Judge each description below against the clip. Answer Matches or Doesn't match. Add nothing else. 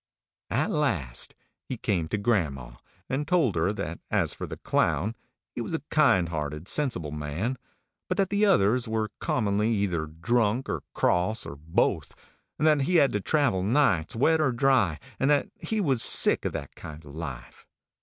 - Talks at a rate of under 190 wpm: Matches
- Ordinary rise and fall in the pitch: Doesn't match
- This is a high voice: Doesn't match